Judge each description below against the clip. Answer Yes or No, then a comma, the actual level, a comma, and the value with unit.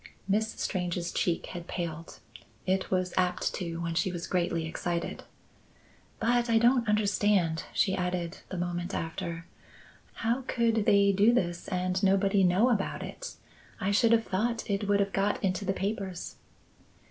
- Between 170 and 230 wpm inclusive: No, average, 155 wpm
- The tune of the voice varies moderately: Yes, average, 3.0 semitones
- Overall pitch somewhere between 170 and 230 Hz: Yes, high, 190 Hz